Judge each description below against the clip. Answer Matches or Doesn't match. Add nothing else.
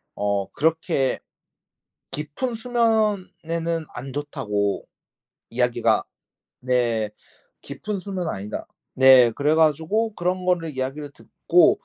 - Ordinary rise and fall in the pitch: Doesn't match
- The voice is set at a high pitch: Doesn't match